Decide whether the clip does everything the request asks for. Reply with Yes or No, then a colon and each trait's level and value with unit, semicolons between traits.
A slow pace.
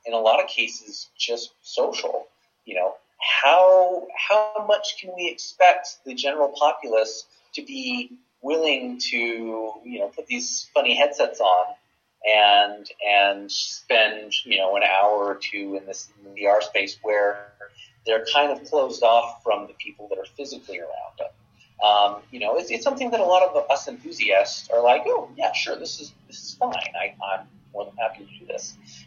No: average, 180 wpm